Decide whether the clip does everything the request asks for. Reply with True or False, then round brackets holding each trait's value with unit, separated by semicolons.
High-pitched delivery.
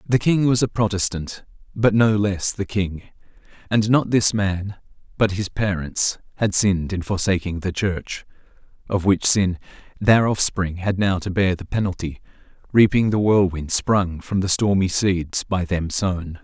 False (95 Hz)